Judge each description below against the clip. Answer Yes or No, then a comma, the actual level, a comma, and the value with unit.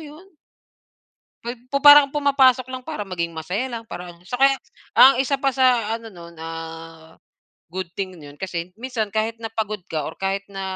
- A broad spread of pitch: Yes, wide, 6.8 semitones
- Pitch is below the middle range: No, high, 220 Hz